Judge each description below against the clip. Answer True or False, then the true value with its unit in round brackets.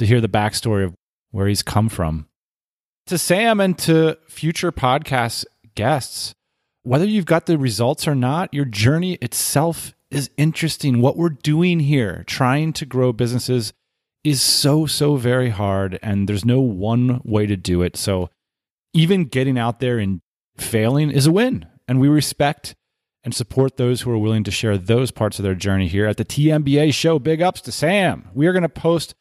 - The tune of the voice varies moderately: False (5.9 semitones)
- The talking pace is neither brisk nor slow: True (185 wpm)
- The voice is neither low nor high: False (130 Hz)